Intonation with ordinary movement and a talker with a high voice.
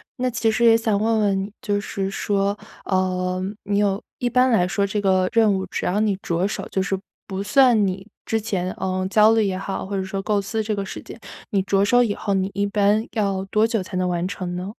No: narrow, 2.3 semitones; high, 200 Hz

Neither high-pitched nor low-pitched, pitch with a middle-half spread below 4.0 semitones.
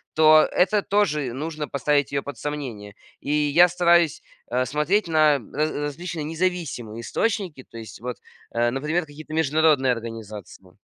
No: medium, 150 Hz; average, 4.4 semitones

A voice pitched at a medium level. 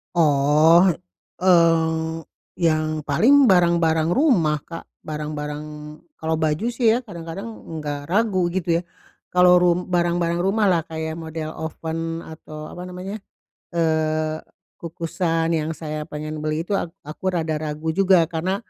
Yes: medium, 165 Hz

